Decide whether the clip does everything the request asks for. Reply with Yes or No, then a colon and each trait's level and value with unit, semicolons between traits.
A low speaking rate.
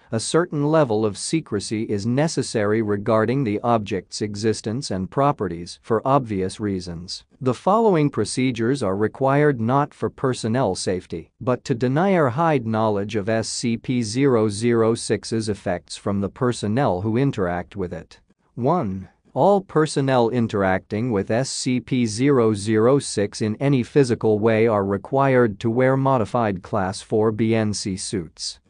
Yes: slow, 125 wpm